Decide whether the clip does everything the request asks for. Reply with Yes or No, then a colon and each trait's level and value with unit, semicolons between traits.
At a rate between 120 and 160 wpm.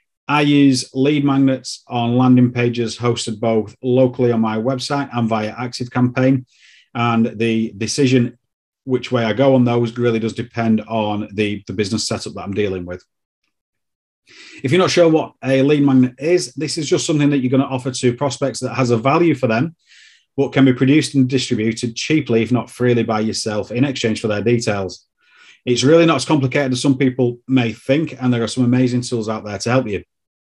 No: average, 200 wpm